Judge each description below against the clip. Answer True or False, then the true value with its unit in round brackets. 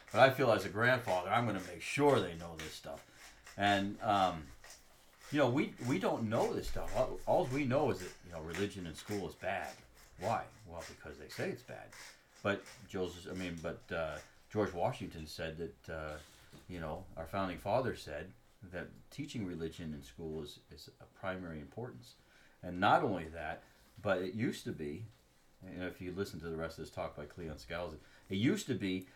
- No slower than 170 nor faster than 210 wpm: True (200 wpm)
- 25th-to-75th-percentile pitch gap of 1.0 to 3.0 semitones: False (3.7 semitones)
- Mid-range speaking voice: False (90 Hz)